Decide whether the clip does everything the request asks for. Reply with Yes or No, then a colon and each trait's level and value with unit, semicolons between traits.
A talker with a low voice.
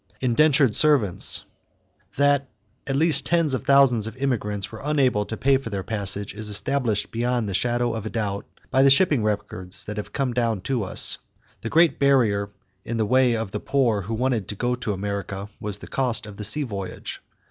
Yes: low, 115 Hz